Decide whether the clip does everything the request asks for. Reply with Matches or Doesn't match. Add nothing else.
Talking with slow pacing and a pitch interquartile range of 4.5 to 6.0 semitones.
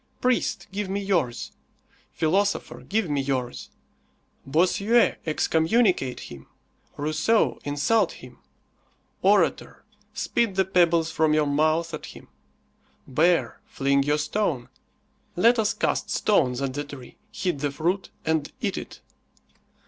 Matches